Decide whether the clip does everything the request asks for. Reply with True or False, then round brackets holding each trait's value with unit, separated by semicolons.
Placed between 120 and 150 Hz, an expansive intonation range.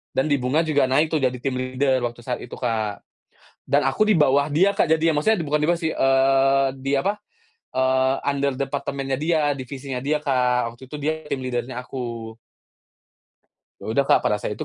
False (135 Hz; 2.6 semitones)